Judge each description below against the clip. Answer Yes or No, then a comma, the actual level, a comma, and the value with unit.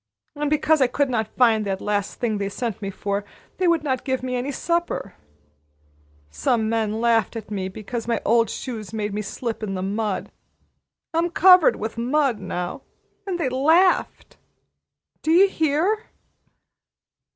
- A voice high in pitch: Yes, high, 235 Hz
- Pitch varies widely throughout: Yes, wide, 6.0 semitones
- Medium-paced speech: Yes, average, 160 wpm